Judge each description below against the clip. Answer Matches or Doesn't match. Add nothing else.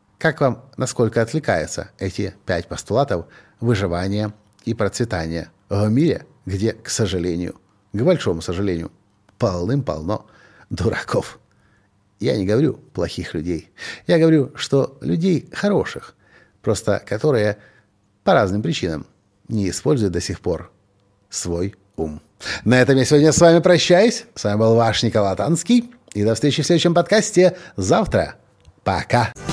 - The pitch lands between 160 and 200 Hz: Doesn't match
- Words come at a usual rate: Matches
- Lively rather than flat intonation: Matches